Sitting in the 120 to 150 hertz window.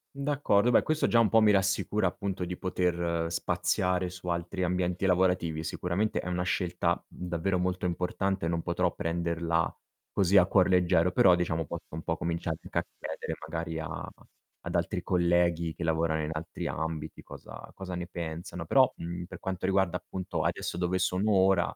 No: very low, 90 Hz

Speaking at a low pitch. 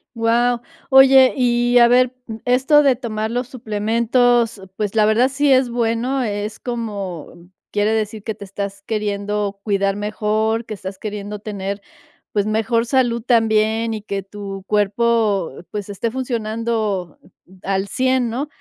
No: high, 220 Hz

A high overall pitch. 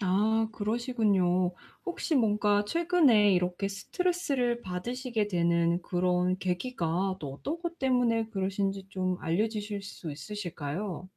Yes: high, 205 Hz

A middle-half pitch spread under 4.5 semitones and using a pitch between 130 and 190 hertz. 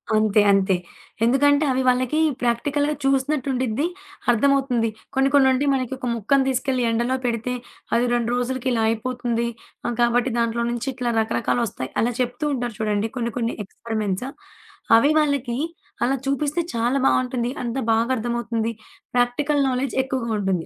No: narrow, 2.4 semitones; high, 245 Hz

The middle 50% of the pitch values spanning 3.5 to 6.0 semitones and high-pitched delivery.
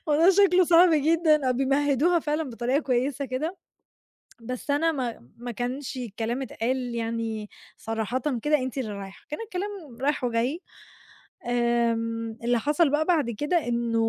Yes: average, 4.5 semitones; very high, 260 Hz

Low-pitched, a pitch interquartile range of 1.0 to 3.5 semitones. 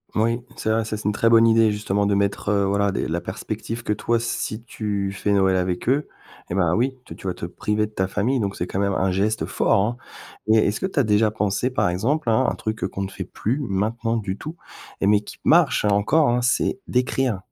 Yes: low, 105 Hz; average, 2.9 semitones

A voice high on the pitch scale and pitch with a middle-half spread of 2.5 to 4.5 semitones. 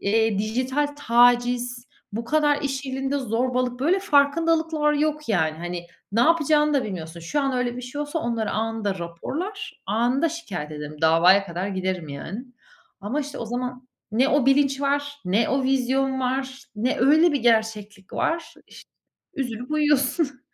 No: very high, 255 Hz; average, 5.0 semitones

